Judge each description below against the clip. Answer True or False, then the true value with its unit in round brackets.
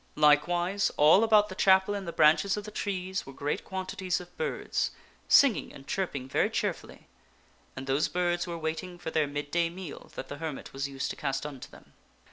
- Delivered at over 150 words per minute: True (195 wpm)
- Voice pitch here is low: False (175 Hz)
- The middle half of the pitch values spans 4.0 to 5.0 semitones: True (4.4 semitones)